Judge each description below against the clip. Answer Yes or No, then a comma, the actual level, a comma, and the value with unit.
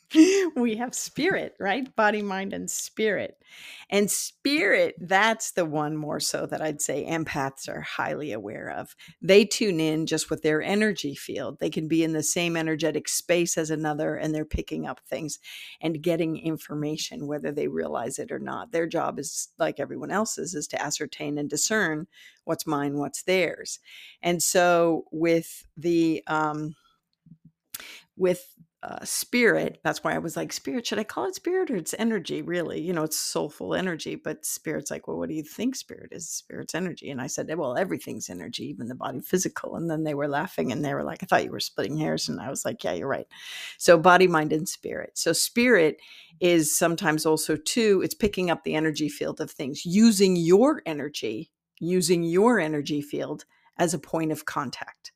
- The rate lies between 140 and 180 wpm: No, average, 190 wpm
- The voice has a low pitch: No, medium, 170 Hz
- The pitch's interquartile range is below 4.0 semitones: No, average, 4.6 semitones